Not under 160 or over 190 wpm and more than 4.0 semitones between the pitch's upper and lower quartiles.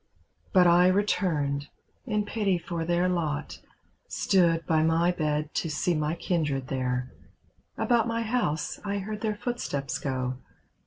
No: average, 140 wpm; average, 5.2 semitones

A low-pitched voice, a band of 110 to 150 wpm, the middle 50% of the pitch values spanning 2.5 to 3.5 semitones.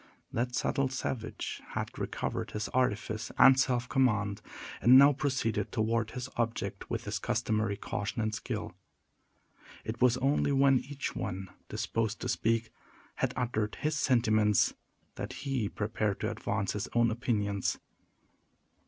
Yes: low, 115 Hz; slow, 135 wpm; average, 3.1 semitones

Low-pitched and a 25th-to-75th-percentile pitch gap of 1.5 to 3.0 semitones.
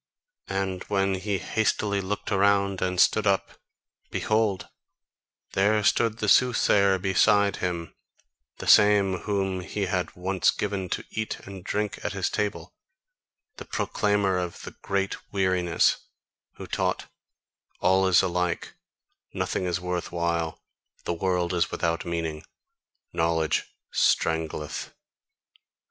Yes: very low, 95 Hz; narrow, 2.4 semitones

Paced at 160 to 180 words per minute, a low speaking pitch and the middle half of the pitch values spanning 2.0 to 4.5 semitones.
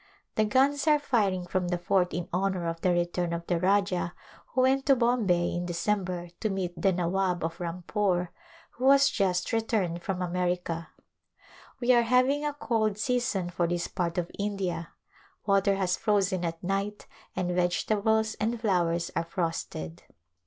No: average, 165 wpm; medium, 185 Hz; average, 3.7 semitones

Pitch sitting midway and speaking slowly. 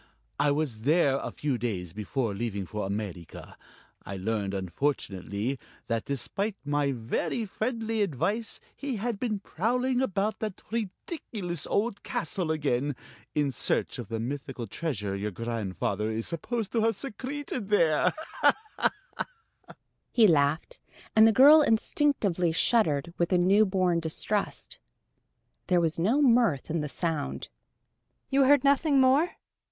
Yes: medium, 170 Hz; slow, 130 wpm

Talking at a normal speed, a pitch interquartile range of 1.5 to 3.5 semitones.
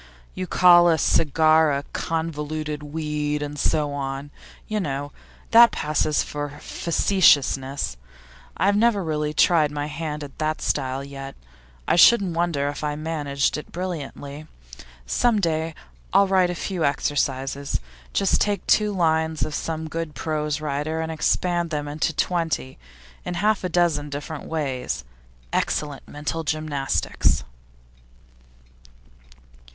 No: slow, 130 wpm; narrow, 2.6 semitones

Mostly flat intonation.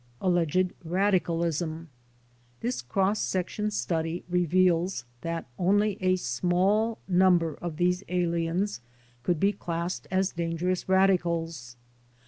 Yes: narrow, 2.1 semitones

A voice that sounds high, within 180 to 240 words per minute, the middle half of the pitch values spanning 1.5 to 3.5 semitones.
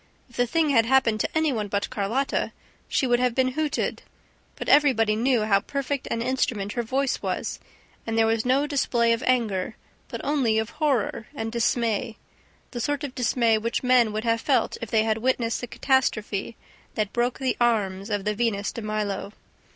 Yes: high, 235 Hz; average, 190 wpm; average, 3.2 semitones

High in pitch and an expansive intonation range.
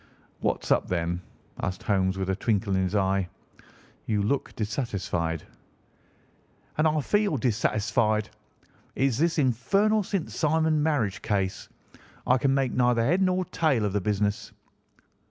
No: low, 115 Hz; wide, 7.5 semitones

